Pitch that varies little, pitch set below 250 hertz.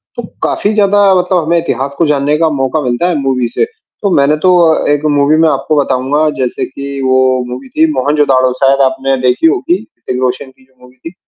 No: average, 3.7 semitones; medium, 140 Hz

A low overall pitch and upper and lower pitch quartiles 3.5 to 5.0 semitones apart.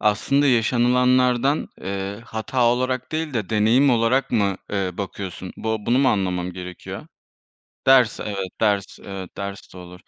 Yes: low, 110 Hz; average, 4.4 semitones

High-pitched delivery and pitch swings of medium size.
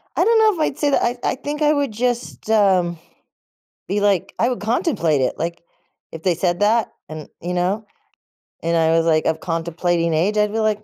No: high, 205 Hz; wide, 6.1 semitones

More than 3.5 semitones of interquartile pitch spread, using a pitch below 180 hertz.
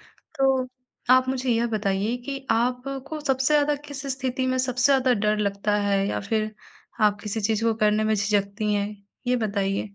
No: average, 3.9 semitones; high, 230 Hz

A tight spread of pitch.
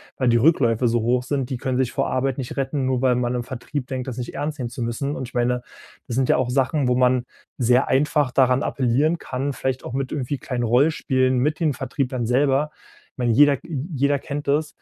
Yes: narrow, 2.2 semitones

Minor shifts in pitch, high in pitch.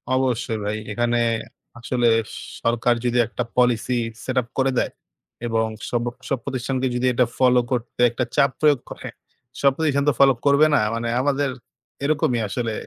No: narrow, 2.3 semitones; low, 125 Hz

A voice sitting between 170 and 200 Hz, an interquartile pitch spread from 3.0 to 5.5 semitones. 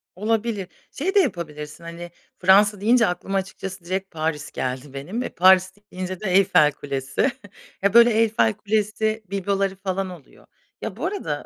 Yes: high, 190 Hz; average, 3.8 semitones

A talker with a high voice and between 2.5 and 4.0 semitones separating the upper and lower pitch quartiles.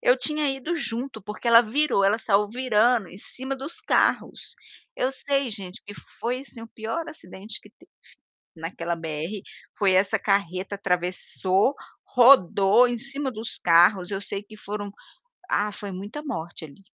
No: high, 210 Hz; average, 4.7 semitones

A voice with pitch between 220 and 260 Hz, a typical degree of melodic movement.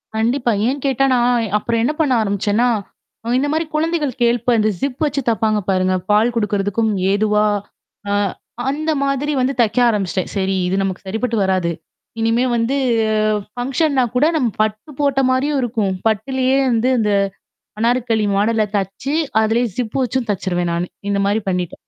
Yes: high, 230 Hz; average, 4.2 semitones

